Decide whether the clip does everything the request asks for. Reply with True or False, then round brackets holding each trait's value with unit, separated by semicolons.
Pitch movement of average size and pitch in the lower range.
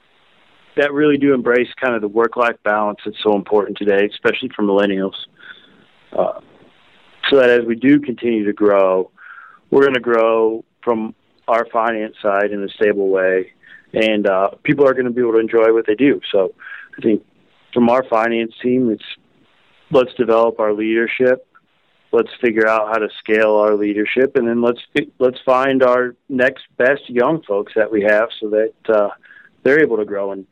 True (3.0 semitones; 115 Hz)